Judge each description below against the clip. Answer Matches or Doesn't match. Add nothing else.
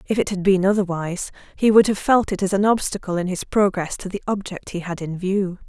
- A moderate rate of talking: Doesn't match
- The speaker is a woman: Matches